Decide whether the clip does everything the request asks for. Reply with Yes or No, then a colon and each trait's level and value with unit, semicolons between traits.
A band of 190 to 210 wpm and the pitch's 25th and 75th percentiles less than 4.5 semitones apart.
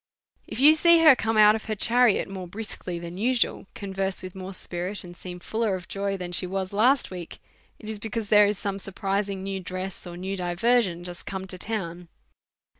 Yes: fast, 205 wpm; average, 3.0 semitones